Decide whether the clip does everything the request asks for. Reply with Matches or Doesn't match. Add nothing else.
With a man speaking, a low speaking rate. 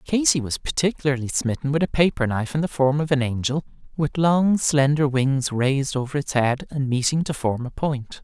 Doesn't match